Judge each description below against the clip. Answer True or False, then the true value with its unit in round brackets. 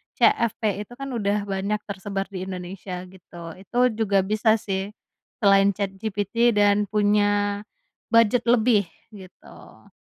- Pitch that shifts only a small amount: True (1.9 semitones)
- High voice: True (205 Hz)